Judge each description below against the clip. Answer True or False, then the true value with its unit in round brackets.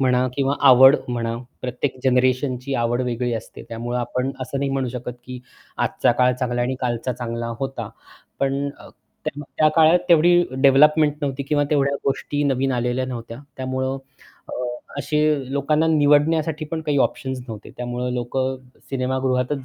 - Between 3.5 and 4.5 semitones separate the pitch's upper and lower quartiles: False (2.7 semitones)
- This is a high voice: False (130 Hz)